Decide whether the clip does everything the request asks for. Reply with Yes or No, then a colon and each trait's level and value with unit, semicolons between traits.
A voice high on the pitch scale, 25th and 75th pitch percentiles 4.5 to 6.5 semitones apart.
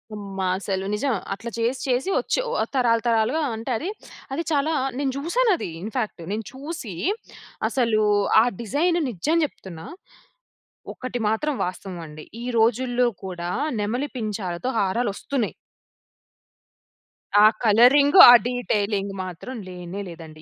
Yes: high, 225 Hz; average, 5.2 semitones